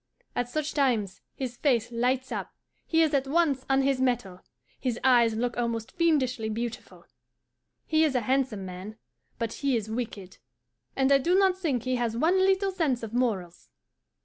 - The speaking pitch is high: Yes, very high, 250 Hz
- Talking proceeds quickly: No, average, 175 wpm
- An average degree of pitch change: Yes, average, 3.8 semitones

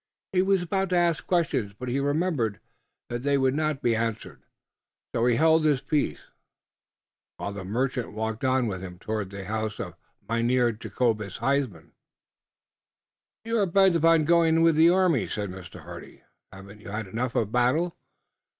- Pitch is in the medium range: No, low, 125 Hz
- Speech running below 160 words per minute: No, average, 170 wpm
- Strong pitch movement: Yes, wide, 7.1 semitones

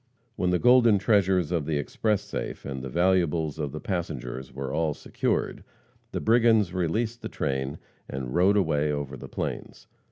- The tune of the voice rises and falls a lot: Yes, wide, 6.0 semitones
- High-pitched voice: No, very low, 85 Hz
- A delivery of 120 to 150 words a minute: No, average, 165 wpm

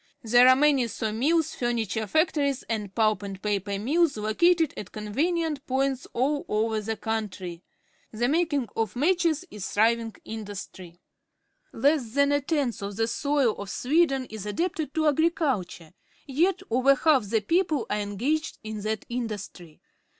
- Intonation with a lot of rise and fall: Yes, wide, 5.8 semitones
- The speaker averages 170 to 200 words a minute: No, average, 155 wpm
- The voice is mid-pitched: No, high, 240 Hz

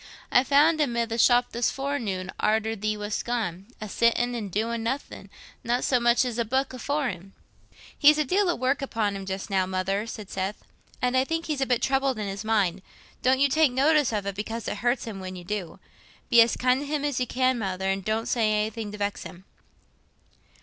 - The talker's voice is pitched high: Yes, high, 230 Hz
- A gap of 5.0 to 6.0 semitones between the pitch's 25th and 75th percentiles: No, average, 4.3 semitones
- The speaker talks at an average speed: No, fast, 220 wpm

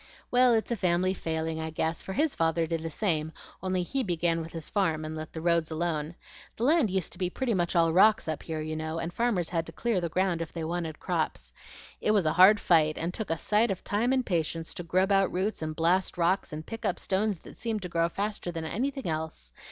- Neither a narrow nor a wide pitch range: Yes, average, 3.8 semitones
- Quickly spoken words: Yes, fast, 245 wpm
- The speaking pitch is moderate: Yes, medium, 175 Hz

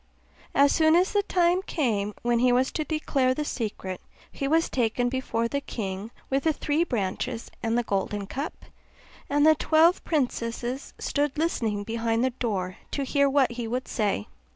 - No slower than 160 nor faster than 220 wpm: Yes, average, 175 wpm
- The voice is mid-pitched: No, very high, 255 Hz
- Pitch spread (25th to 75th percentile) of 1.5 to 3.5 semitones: No, average, 4.7 semitones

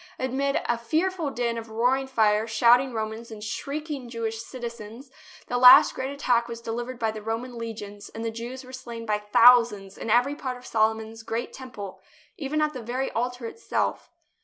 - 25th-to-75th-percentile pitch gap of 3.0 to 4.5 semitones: No, narrow, 2.6 semitones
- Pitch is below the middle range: No, high, 235 Hz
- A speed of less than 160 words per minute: No, average, 180 wpm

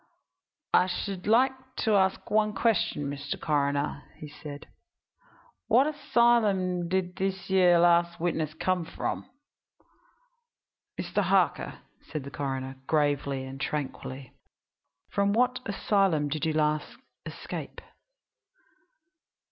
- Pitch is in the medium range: Yes, medium, 175 Hz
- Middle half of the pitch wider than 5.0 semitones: Yes, wide, 5.5 semitones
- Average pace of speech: No, slow, 110 wpm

